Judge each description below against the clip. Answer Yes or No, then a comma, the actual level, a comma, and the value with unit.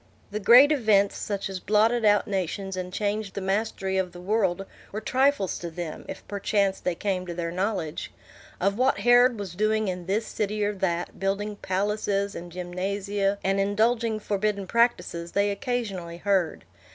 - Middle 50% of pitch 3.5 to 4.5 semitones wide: No, narrow, 2.4 semitones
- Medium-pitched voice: No, high, 200 Hz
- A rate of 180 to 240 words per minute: No, average, 165 wpm